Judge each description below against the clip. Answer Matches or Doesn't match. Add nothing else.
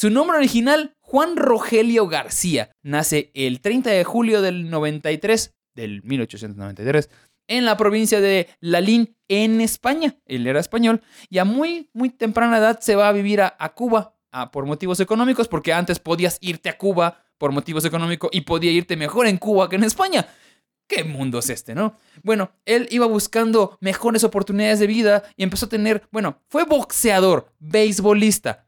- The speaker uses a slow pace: Doesn't match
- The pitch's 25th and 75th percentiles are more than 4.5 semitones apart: Matches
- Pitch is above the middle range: Matches